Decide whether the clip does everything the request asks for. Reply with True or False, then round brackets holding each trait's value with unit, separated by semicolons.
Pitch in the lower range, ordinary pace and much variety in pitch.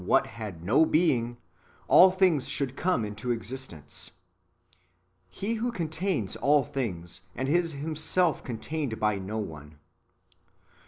False (130 Hz; 120 wpm; 7.2 semitones)